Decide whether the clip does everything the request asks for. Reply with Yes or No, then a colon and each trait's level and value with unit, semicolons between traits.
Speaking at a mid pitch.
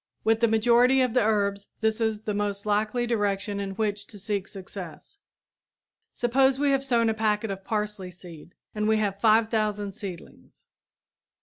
No: high, 215 Hz